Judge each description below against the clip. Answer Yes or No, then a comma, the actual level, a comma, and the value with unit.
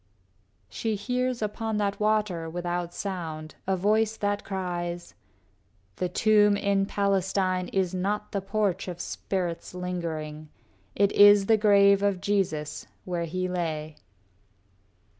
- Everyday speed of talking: No, slow, 125 wpm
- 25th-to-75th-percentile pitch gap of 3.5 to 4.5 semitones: No, average, 3.0 semitones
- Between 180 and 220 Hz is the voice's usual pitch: Yes, high, 190 Hz